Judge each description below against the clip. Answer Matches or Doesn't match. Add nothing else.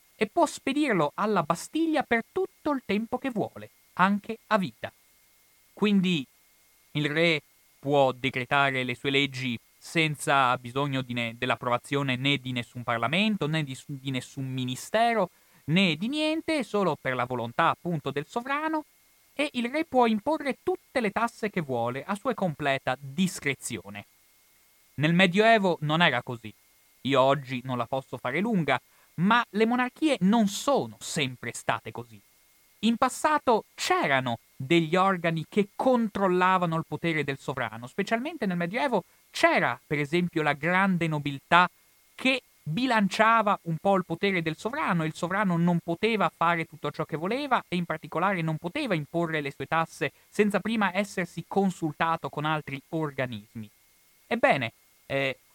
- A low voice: Doesn't match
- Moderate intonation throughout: Doesn't match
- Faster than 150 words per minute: Doesn't match